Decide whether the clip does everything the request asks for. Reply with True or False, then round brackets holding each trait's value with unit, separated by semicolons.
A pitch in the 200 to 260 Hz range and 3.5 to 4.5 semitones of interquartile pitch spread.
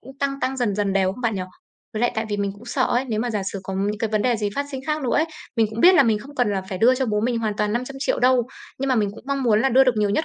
True (230 Hz; 3.9 semitones)